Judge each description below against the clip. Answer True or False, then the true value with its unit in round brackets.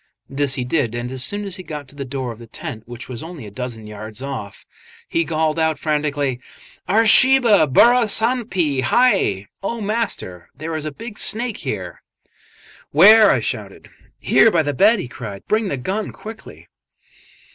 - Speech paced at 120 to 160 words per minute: False (180 wpm)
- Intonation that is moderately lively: False (8.9 semitones)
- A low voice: False (155 Hz)